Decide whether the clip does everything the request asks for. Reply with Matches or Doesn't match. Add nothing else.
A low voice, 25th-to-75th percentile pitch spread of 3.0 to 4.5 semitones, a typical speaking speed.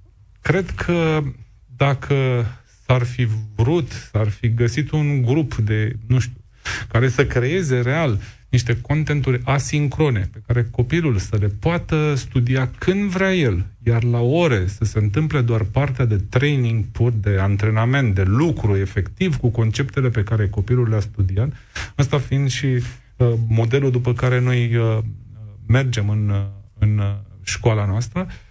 Matches